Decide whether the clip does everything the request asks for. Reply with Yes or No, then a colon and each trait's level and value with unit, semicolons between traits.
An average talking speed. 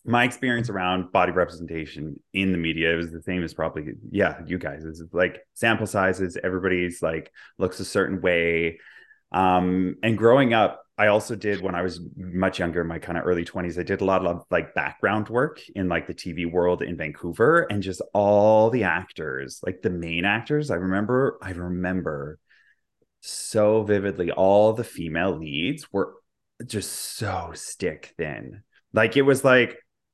Yes: average, 170 wpm